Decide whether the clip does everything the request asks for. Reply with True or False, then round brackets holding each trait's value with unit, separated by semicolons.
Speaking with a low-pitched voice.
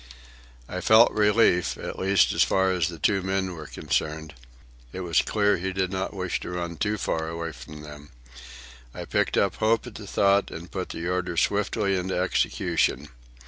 True (90 Hz)